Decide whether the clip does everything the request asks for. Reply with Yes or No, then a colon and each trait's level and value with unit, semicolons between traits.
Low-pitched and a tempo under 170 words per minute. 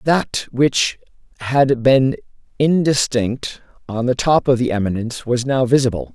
Yes: low, 125 Hz; slow, 135 wpm